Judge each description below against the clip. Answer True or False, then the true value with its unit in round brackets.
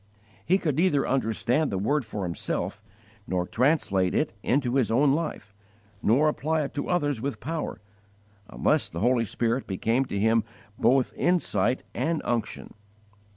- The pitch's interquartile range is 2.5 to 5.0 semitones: False (5.4 semitones)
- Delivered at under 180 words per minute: True (150 wpm)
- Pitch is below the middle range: True (125 Hz)